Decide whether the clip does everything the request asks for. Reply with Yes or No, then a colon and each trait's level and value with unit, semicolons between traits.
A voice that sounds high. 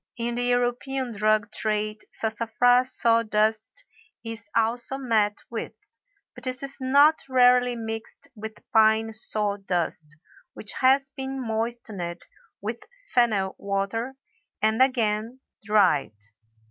Yes: high, 225 Hz